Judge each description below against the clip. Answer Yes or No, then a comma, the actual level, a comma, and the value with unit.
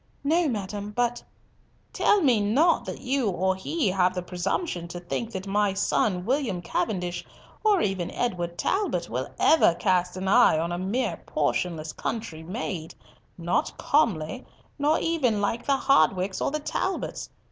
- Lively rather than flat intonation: Yes, wide, 6.4 semitones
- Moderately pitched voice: No, high, 200 Hz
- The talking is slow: No, average, 155 wpm